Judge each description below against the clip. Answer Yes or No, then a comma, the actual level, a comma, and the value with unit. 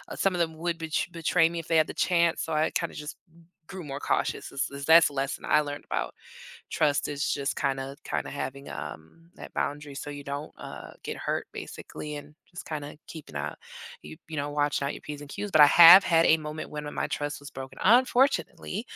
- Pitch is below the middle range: No, medium, 150 Hz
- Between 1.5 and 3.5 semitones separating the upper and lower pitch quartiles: Yes, average, 2.7 semitones